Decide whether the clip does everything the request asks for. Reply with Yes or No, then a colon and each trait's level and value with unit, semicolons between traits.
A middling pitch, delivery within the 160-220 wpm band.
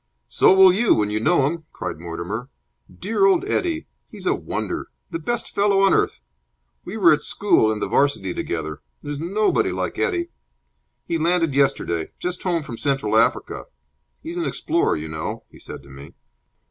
Yes: medium, 160 Hz; average, 175 wpm